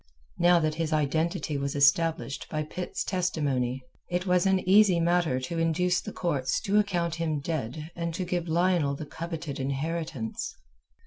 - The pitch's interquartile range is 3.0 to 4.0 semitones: Yes, average, 3.4 semitones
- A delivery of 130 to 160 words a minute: Yes, average, 155 wpm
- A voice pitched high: No, medium, 165 Hz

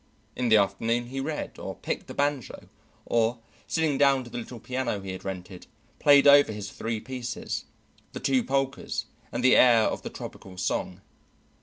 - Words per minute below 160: No, average, 175 wpm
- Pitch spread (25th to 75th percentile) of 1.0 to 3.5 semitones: No, average, 4.0 semitones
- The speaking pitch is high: No, low, 120 Hz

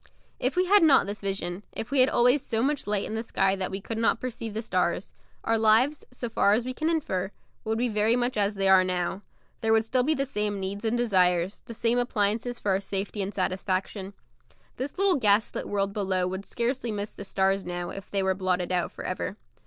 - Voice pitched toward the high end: Yes, high, 210 Hz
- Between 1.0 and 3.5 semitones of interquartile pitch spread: No, average, 3.9 semitones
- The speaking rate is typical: No, fast, 225 wpm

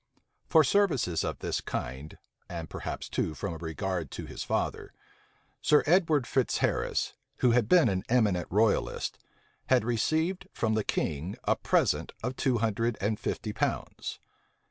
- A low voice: Yes, low, 110 Hz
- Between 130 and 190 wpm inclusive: Yes, average, 150 wpm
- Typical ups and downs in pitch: No, wide, 6.4 semitones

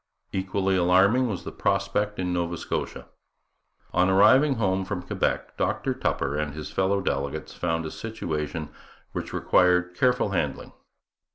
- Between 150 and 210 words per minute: No, average, 140 wpm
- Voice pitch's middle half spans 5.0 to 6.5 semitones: No, average, 3.2 semitones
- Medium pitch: No, very low, 95 Hz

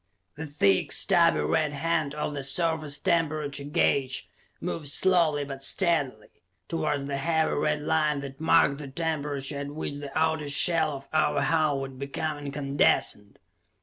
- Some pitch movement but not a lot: No, narrow, 2.2 semitones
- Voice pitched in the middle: Yes, medium, 145 Hz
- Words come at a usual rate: Yes, average, 150 wpm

